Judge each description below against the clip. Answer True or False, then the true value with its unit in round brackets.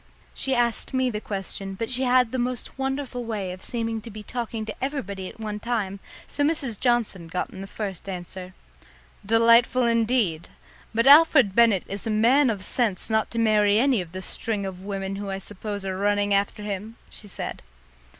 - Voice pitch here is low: False (215 Hz)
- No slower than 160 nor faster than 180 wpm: False (190 wpm)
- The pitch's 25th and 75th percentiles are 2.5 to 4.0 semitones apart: True (3.6 semitones)